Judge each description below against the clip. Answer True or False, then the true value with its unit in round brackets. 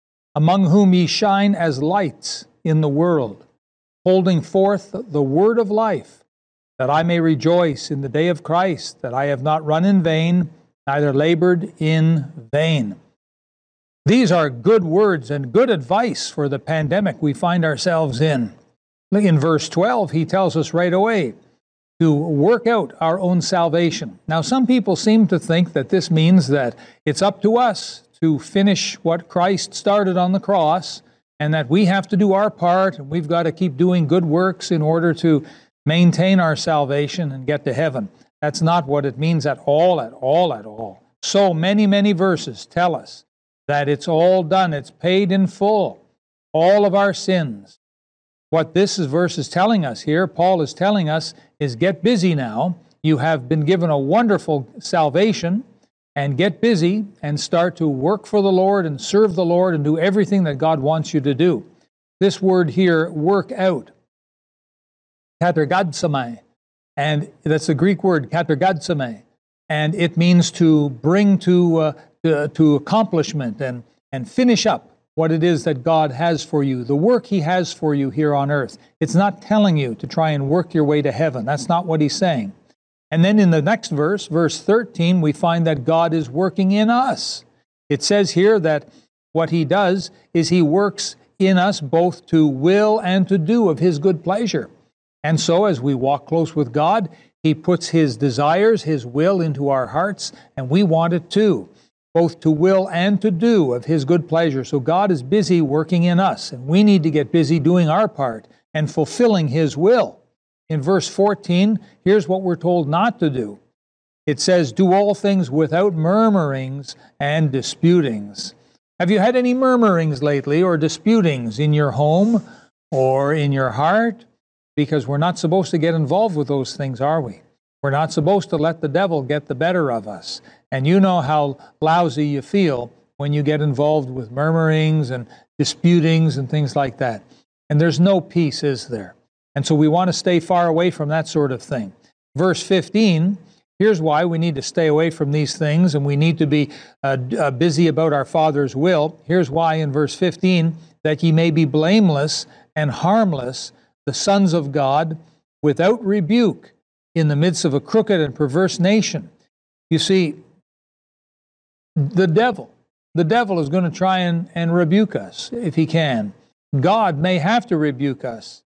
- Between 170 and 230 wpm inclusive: True (180 wpm)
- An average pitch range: True (3.9 semitones)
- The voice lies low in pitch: False (165 Hz)